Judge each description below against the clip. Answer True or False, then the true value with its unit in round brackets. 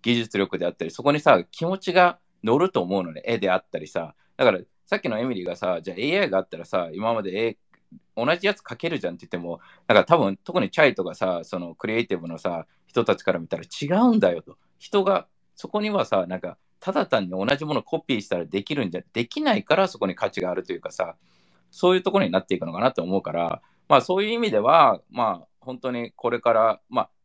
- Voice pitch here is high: False (140 Hz)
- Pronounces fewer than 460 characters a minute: True (450 characters per minute)